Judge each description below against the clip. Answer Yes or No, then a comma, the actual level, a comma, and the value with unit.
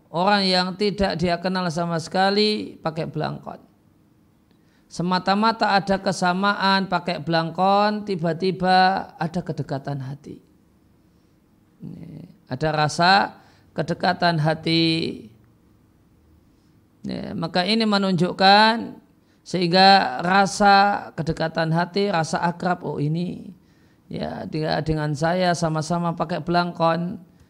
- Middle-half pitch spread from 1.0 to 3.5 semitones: Yes, average, 3.0 semitones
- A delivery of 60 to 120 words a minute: Yes, slow, 85 wpm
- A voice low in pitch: No, medium, 180 Hz